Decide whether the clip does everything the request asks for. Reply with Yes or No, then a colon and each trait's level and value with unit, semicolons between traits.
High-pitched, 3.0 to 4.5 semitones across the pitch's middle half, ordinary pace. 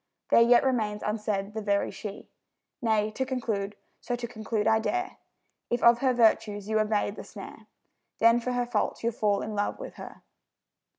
No: high, 220 Hz; narrow, 2.4 semitones; average, 180 wpm